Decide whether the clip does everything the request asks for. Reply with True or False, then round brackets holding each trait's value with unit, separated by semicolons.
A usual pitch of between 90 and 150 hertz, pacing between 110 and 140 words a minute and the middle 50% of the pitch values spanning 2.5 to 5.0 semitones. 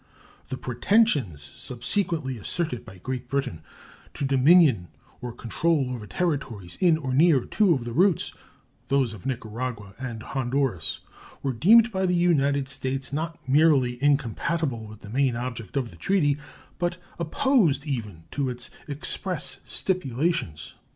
False (135 Hz; 135 wpm; 5.5 semitones)